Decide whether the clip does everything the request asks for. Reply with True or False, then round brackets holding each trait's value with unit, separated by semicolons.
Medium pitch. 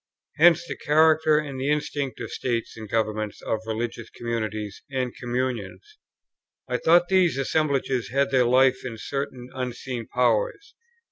False (130 Hz)